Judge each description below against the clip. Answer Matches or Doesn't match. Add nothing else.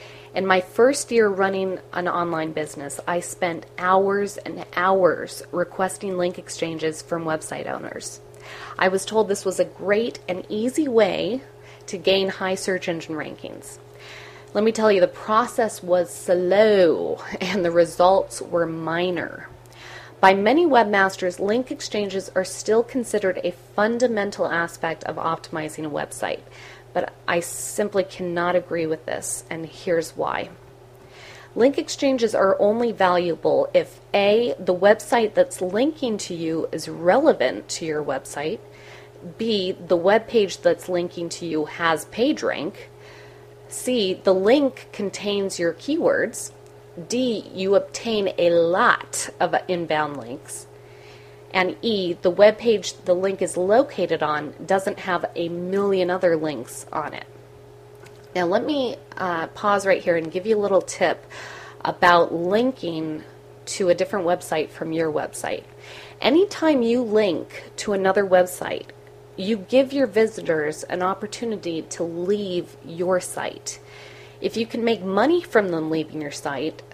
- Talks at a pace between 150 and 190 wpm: Doesn't match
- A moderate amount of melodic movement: Matches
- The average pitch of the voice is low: Doesn't match